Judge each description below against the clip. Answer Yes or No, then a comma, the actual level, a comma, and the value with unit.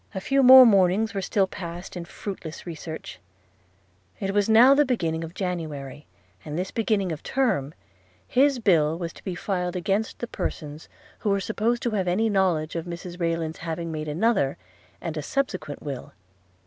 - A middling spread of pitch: Yes, average, 4.9 semitones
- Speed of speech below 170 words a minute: No, average, 175 wpm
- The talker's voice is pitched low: No, medium, 180 Hz